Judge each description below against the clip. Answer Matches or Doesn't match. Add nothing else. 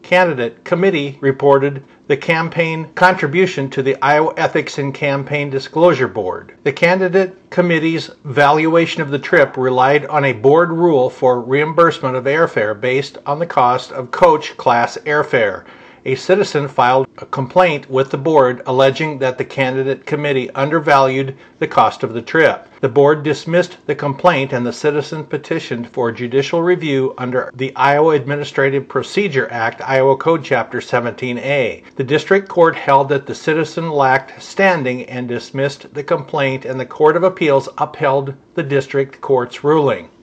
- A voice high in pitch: Doesn't match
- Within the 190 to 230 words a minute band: Doesn't match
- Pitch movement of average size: Matches